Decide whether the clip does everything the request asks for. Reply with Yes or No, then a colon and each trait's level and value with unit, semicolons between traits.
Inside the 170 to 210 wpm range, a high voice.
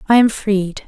Yes: fast, 205 wpm; high, 205 Hz